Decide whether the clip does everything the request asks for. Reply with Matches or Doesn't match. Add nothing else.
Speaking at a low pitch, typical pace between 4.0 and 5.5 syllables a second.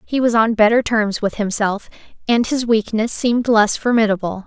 Doesn't match